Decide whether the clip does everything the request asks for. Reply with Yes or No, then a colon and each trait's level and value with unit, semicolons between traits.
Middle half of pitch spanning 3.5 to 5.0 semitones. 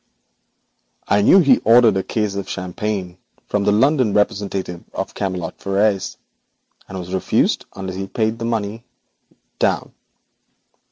No: narrow, 2.6 semitones